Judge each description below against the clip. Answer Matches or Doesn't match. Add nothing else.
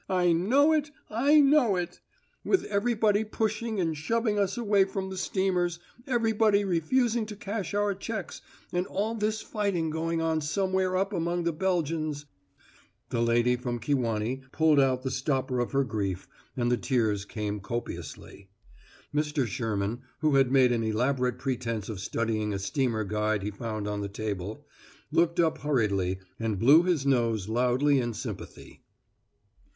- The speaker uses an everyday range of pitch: Doesn't match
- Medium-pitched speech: Matches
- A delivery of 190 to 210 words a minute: Doesn't match